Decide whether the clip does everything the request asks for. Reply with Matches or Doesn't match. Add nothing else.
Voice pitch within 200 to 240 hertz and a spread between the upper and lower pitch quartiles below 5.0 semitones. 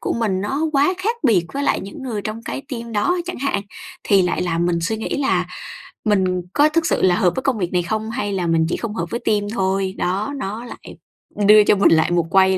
Matches